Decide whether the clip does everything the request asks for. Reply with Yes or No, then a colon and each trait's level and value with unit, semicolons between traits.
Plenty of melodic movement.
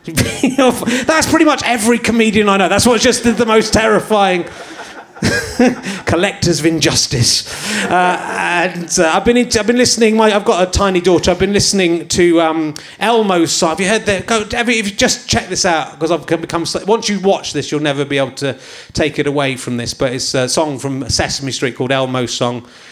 Yes: wide, 7.5 semitones